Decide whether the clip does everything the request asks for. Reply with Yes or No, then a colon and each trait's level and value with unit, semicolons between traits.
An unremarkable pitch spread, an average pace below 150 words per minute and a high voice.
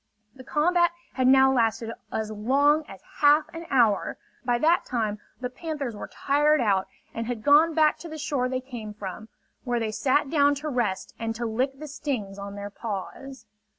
No: average, 4.9 semitones; average, 185 wpm; very high, 255 Hz